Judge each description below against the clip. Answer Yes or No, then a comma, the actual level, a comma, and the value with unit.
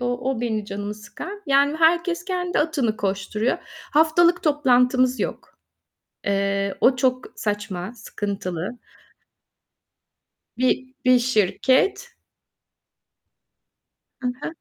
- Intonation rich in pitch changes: Yes, wide, 6.2 semitones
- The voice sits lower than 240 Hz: No, very high, 250 Hz